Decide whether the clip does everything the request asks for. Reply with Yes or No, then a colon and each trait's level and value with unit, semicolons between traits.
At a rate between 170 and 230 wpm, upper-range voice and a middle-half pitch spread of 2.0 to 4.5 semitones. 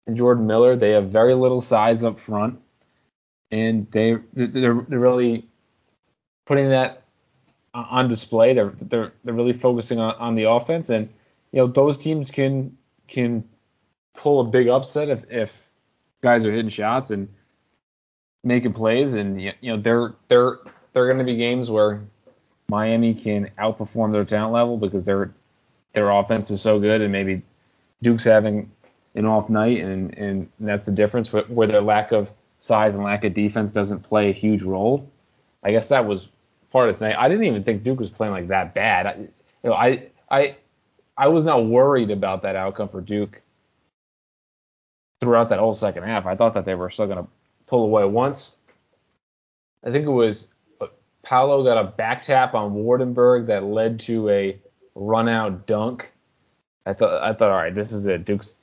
No: average, 180 wpm; low, 110 Hz; average, 3.0 semitones